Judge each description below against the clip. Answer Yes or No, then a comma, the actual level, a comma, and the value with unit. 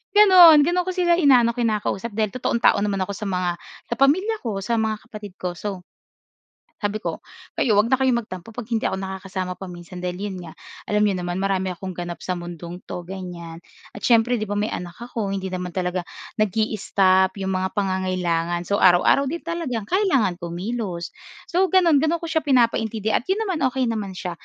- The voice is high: Yes, high, 205 Hz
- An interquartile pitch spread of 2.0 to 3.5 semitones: No, average, 4.9 semitones